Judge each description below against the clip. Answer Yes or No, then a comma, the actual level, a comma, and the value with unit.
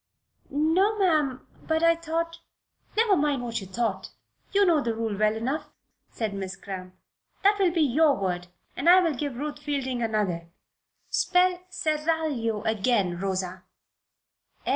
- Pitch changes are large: Yes, wide, 7.5 semitones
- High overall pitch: Yes, very high, 275 Hz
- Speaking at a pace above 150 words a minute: No, average, 140 wpm